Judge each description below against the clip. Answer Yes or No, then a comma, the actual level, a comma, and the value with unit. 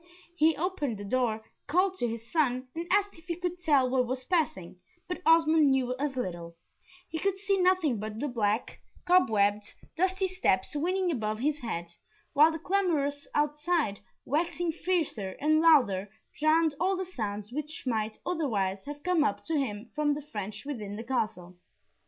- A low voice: No, very high, 290 Hz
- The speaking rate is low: No, average, 170 wpm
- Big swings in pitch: Yes, wide, 7.5 semitones